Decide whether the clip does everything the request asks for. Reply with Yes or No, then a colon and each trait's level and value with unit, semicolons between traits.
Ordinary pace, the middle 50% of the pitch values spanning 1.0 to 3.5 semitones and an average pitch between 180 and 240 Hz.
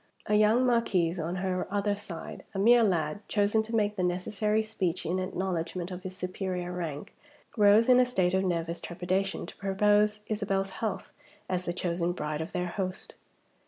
Yes: average, 175 wpm; average, 2.8 semitones; high, 190 Hz